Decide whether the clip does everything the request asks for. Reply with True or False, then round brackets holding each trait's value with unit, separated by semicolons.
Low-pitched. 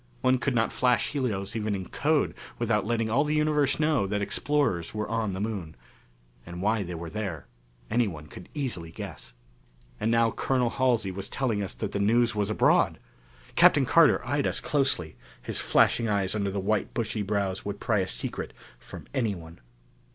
True (110 Hz)